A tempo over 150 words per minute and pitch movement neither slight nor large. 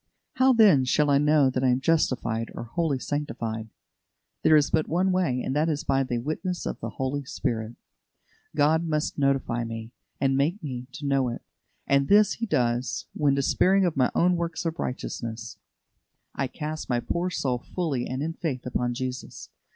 Yes: average, 180 wpm; average, 4.4 semitones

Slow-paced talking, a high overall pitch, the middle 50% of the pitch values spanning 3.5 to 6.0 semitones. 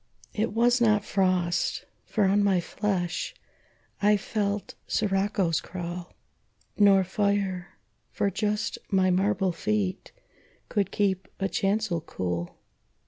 No: slow, 110 wpm; high, 195 Hz; narrow, 2.4 semitones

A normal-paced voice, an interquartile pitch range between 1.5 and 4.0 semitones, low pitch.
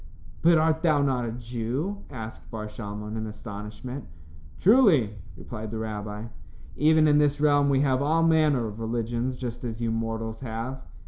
No: average, 165 wpm; average, 4.6 semitones; low, 120 Hz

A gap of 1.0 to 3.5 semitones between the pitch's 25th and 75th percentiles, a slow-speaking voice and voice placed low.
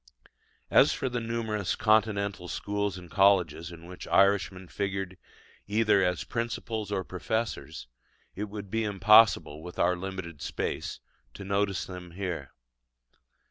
Yes: average, 2.9 semitones; slow, 130 wpm; low, 100 Hz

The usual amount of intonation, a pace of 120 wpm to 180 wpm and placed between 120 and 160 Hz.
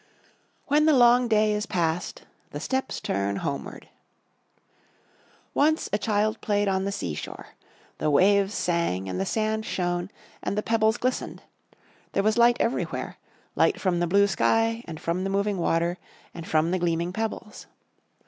No: average, 4.4 semitones; average, 160 wpm; high, 200 Hz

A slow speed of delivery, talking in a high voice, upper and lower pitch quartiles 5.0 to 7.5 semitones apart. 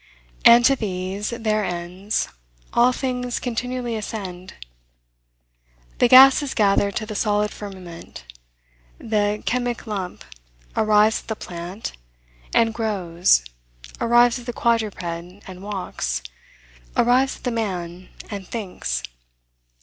No: slow, 110 wpm; high, 210 Hz; average, 4.3 semitones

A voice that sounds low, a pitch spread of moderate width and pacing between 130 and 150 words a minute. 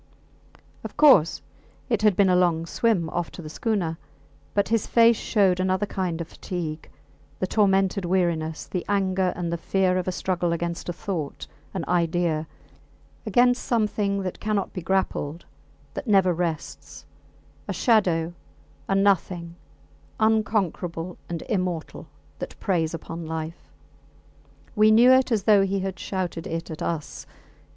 No: medium, 185 Hz; average, 3.2 semitones; average, 145 wpm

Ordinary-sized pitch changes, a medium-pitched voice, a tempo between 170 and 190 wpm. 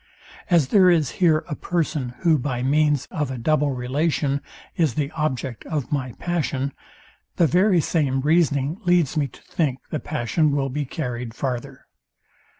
No: average, 3.5 semitones; medium, 145 Hz; average, 155 wpm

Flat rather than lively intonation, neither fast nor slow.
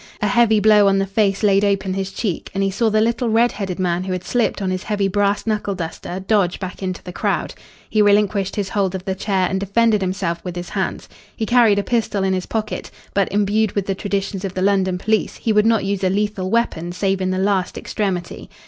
No: narrow, 2.0 semitones; fast, 235 wpm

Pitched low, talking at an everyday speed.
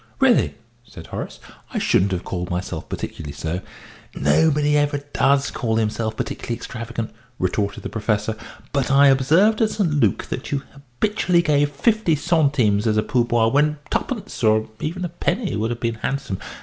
Yes: low, 130 Hz; average, 160 wpm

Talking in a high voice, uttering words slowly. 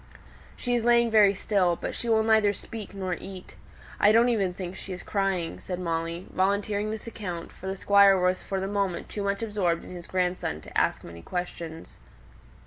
No: high, 195 Hz; average, 195 wpm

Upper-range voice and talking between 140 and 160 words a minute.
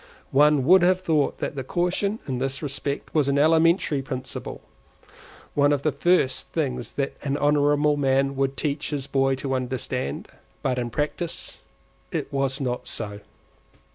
No: medium, 140 Hz; average, 145 wpm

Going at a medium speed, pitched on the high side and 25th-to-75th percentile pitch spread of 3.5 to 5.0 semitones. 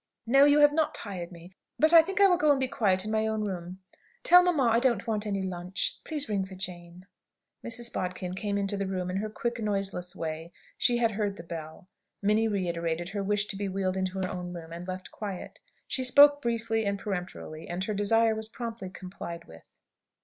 No: fast, 215 wpm; high, 200 Hz; average, 3.9 semitones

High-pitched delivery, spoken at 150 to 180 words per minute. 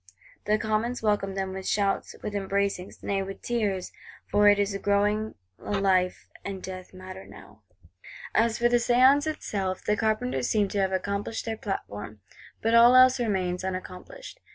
Yes: high, 200 Hz; average, 160 wpm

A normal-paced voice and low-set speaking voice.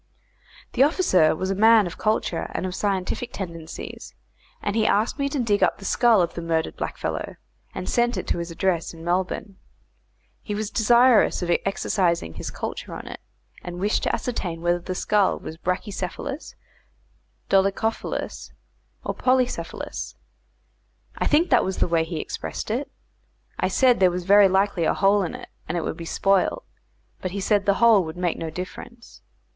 No: average, 175 wpm; high, 195 Hz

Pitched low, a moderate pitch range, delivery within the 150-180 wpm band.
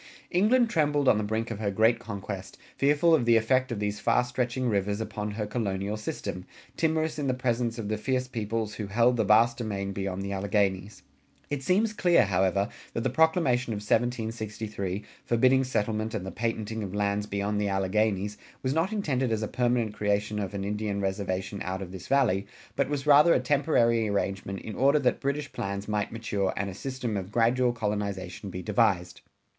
No: low, 110 Hz; average, 4.1 semitones; average, 190 wpm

